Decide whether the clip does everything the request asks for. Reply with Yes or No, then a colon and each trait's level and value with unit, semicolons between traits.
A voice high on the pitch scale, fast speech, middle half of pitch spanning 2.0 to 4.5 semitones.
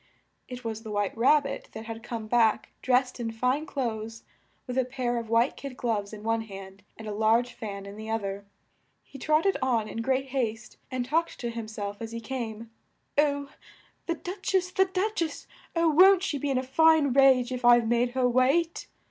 Yes: high, 245 Hz; fast, 210 wpm; average, 3.8 semitones